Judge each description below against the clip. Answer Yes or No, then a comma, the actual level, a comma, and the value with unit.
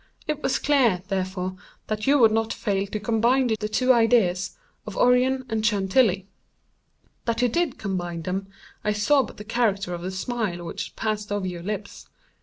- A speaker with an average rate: Yes, average, 175 wpm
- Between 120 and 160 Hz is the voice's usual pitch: No, high, 210 Hz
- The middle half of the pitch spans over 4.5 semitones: No, average, 4.2 semitones